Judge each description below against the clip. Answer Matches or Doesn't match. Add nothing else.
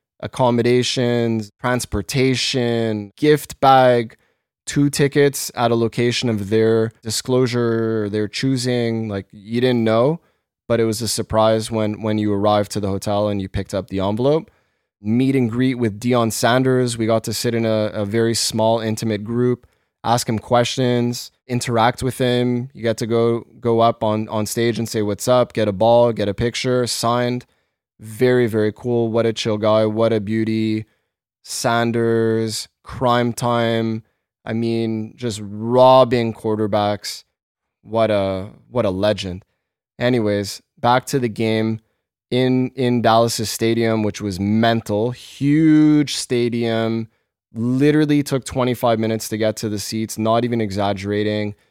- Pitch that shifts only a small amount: Matches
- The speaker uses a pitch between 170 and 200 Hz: Doesn't match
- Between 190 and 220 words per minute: Doesn't match